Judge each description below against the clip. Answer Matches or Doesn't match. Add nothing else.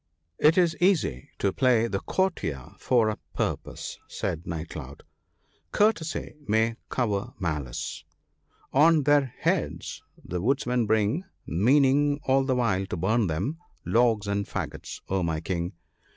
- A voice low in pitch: Matches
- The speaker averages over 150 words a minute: Doesn't match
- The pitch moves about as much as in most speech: Doesn't match